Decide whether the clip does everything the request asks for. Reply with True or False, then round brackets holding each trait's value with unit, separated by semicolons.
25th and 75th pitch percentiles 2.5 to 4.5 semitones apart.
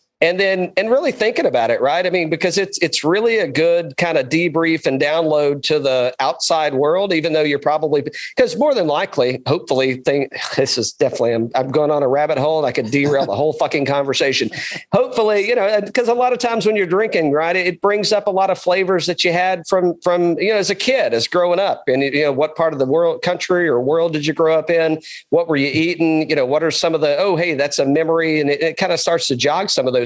True (3.9 semitones)